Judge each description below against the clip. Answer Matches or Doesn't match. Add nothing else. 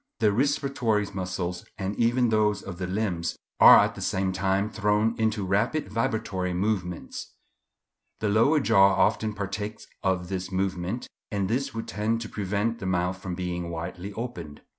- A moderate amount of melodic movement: Matches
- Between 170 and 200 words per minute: Doesn't match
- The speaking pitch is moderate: Doesn't match